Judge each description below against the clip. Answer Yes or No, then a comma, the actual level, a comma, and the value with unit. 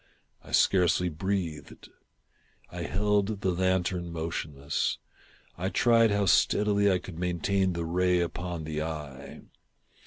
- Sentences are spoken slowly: Yes, slow, 120 wpm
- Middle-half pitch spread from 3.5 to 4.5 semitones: No, average, 3.0 semitones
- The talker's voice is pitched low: Yes, very low, 90 Hz